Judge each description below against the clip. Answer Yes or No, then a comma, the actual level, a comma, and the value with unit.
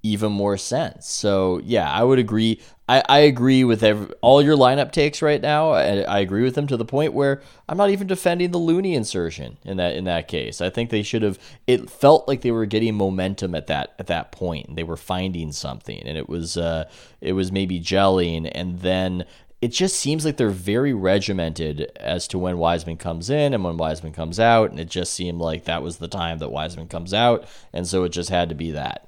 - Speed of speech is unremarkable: No, fast, 225 wpm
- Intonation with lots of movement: Yes, wide, 6.8 semitones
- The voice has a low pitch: Yes, low, 100 Hz